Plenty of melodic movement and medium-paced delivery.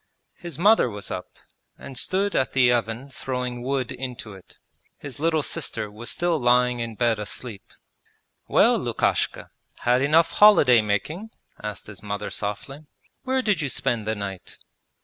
Yes: wide, 5.8 semitones; average, 150 wpm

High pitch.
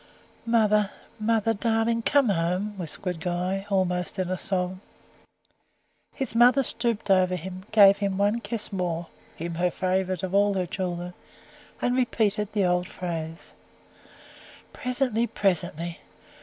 Yes: high, 195 Hz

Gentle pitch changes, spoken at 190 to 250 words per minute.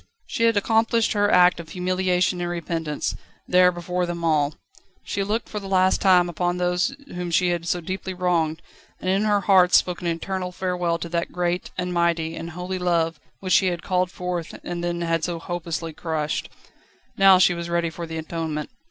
Yes: narrow, 1.5 semitones; average, 195 wpm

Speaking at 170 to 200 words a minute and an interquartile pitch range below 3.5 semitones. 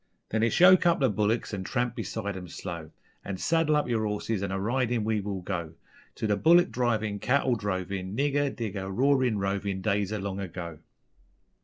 No: average, 185 wpm; average, 4.2 semitones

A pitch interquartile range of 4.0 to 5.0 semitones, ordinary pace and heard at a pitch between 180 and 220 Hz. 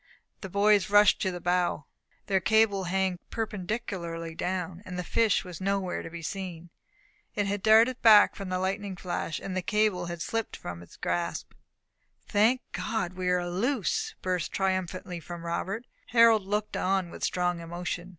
No: average, 2.9 semitones; average, 170 wpm; medium, 185 Hz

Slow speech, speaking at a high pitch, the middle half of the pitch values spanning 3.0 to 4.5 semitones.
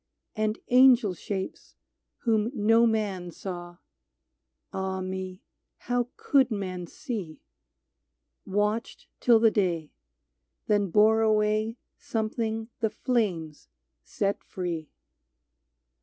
Yes: slow, 100 wpm; high, 210 Hz; average, 3.4 semitones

